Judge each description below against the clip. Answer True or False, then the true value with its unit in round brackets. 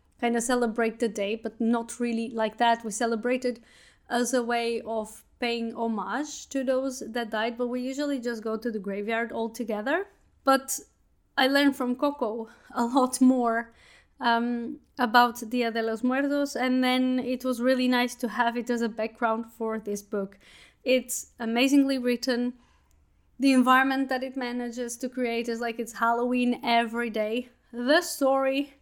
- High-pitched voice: True (240 Hz)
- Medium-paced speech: True (165 wpm)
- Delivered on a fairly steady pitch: True (1.9 semitones)